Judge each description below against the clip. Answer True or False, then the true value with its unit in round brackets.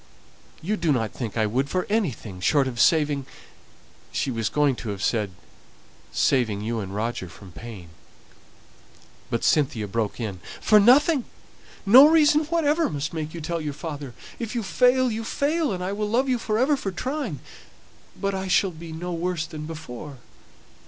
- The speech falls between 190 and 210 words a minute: False (180 wpm)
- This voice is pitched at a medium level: True (160 Hz)